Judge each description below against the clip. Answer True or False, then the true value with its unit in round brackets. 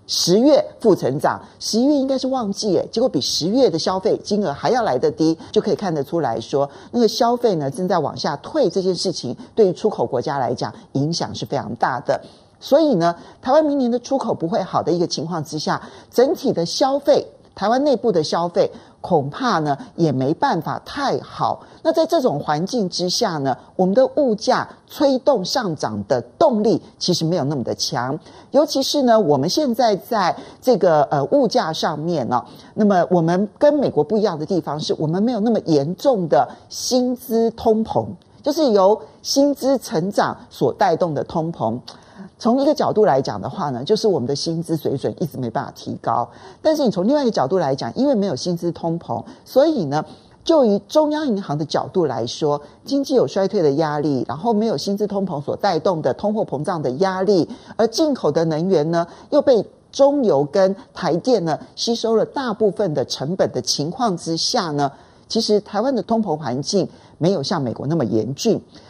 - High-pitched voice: True (200 Hz)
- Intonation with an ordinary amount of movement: False (7.5 semitones)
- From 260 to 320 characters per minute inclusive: True (285 characters per minute)